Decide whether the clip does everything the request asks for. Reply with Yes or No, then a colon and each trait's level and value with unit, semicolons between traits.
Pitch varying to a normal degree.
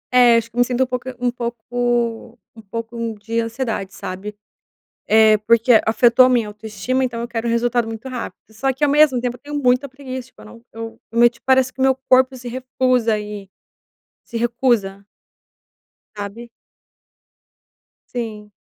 No: narrow, 2.1 semitones